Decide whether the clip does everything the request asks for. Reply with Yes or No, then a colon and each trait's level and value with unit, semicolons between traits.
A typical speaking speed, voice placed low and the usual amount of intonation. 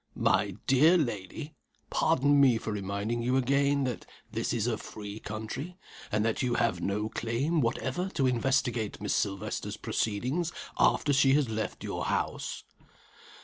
Yes: average, 145 wpm; low, 125 Hz; average, 4.4 semitones